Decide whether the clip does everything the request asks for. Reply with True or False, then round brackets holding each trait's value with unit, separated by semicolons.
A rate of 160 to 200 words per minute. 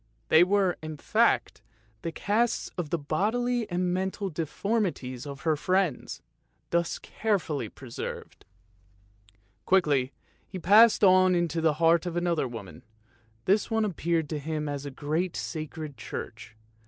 False (135 wpm)